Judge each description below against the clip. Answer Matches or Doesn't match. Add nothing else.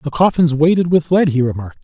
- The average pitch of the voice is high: Doesn't match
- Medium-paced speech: Doesn't match